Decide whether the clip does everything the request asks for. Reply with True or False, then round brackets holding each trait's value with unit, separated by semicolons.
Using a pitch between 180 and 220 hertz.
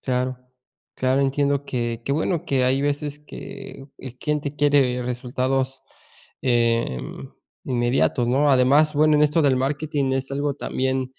False (135 Hz)